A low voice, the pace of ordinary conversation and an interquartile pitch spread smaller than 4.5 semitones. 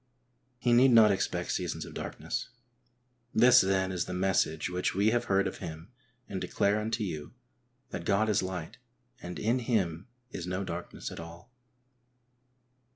Yes: very low, 95 Hz; average, 155 wpm; average, 3.7 semitones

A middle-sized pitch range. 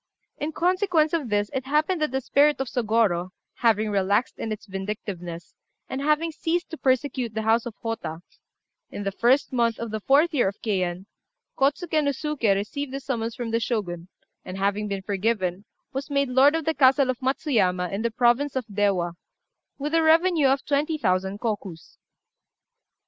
No: wide, 5.9 semitones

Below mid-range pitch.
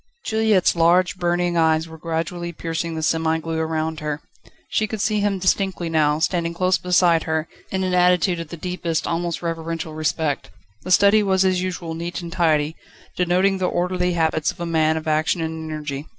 No: medium, 170 Hz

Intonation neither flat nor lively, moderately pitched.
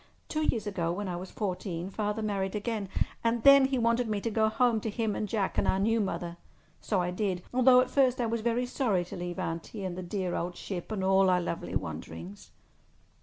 No: average, 4.2 semitones; high, 205 Hz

